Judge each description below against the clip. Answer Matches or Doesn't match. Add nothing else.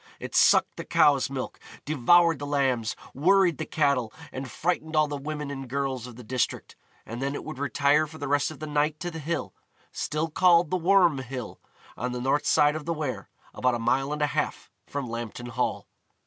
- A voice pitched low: Doesn't match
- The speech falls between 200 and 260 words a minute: Matches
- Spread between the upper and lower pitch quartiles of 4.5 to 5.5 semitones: Doesn't match